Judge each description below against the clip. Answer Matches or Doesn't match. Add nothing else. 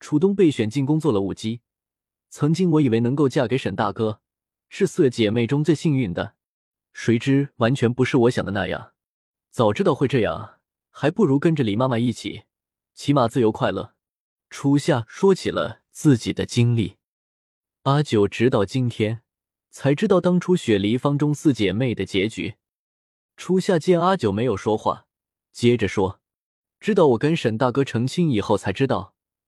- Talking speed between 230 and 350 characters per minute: Matches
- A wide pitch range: Matches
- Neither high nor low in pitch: Doesn't match